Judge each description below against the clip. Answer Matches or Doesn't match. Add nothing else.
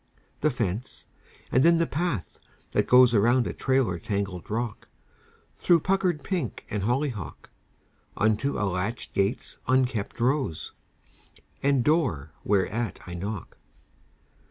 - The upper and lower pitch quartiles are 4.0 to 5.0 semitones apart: Doesn't match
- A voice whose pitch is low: Matches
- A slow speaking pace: Matches